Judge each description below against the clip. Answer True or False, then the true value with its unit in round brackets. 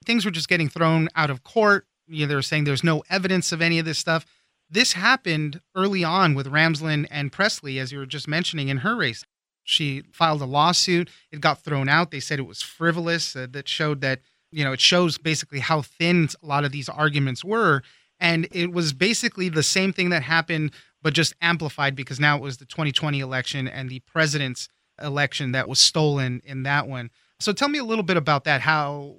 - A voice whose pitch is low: False (155 Hz)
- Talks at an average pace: False (215 wpm)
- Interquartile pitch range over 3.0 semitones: True (3.4 semitones)